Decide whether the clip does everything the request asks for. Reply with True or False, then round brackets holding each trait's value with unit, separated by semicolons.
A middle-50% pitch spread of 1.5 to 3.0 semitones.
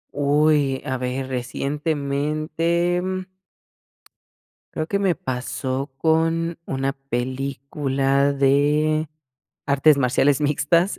True (2.7 semitones)